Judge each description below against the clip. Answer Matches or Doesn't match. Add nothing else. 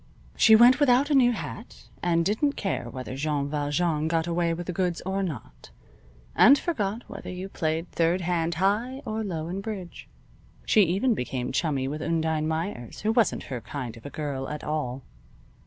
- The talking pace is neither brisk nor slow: Matches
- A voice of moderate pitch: Matches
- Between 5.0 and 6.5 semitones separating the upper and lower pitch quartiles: Matches